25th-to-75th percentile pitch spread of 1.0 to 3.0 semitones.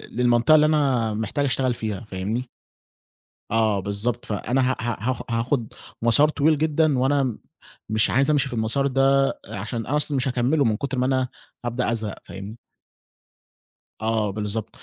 No: average, 3.8 semitones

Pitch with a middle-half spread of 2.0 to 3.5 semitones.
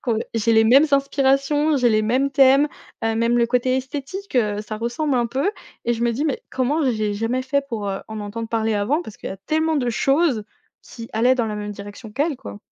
No: average, 4.0 semitones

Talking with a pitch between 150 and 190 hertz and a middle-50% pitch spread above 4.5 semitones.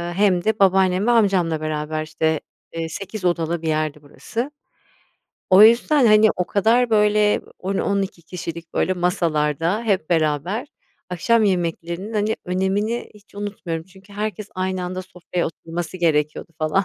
No: medium, 185 Hz; average, 4.0 semitones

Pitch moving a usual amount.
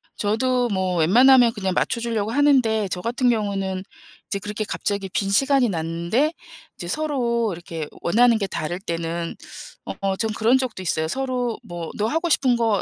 Yes: average, 4.8 semitones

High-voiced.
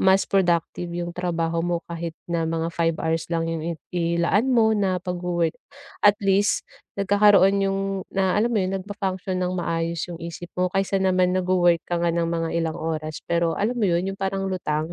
No: medium, 175 Hz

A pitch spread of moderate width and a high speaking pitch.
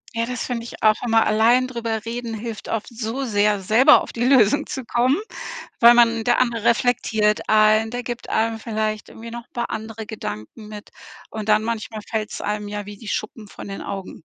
No: narrow, 1.9 semitones; high, 225 Hz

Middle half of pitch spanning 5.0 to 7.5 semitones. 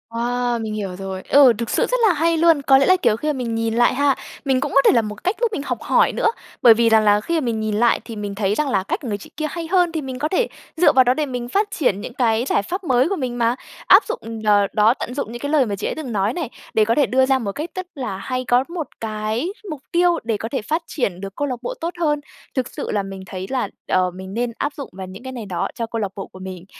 Yes: wide, 5.4 semitones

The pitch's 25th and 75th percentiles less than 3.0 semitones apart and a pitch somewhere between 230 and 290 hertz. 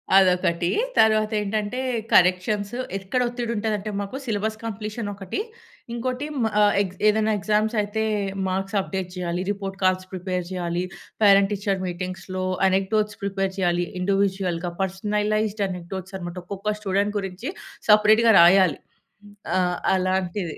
No: narrow, 2.4 semitones; high, 195 Hz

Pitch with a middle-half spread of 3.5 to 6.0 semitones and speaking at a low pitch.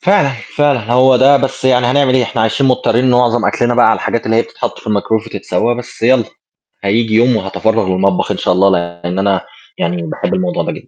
Yes: average, 4.5 semitones; low, 115 Hz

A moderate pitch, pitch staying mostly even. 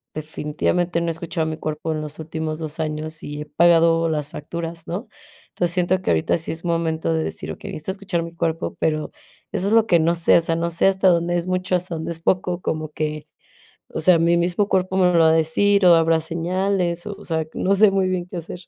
Yes: medium, 170 Hz; narrow, 2.1 semitones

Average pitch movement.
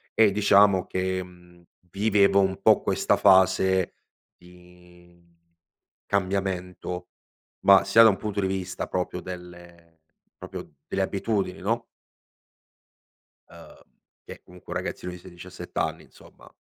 No: narrow, 1.8 semitones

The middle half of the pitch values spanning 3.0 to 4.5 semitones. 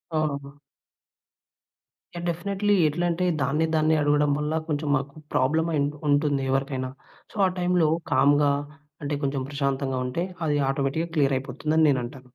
No: narrow, 2.6 semitones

